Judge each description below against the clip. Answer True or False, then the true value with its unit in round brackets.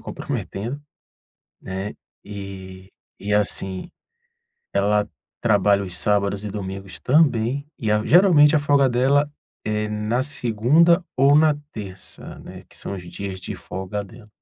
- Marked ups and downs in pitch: True (5.7 semitones)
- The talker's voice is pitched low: True (105 Hz)